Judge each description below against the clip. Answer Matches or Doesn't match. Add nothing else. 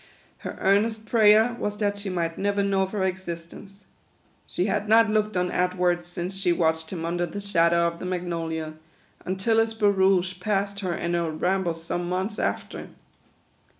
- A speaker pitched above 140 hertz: Matches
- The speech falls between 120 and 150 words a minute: Doesn't match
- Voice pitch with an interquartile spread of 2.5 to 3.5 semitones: Matches